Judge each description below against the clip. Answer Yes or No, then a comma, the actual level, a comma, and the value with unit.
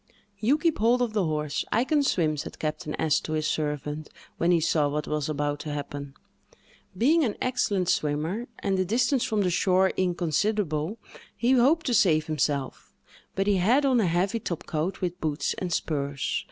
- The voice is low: No, medium, 175 Hz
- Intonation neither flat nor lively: No, wide, 6.5 semitones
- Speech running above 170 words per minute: Yes, average, 180 wpm